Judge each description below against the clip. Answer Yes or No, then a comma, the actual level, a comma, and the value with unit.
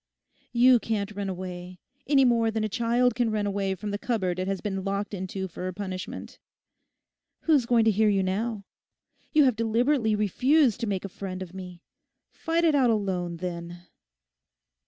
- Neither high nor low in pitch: No, high, 205 Hz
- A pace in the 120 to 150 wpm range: No, average, 175 wpm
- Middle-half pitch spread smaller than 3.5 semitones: No, average, 4.0 semitones